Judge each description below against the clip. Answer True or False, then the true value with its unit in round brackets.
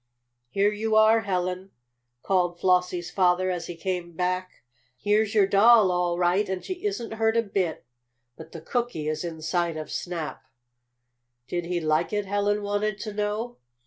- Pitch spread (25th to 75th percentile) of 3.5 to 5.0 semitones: False (3.1 semitones)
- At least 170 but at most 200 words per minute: False (160 wpm)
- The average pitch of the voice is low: False (185 Hz)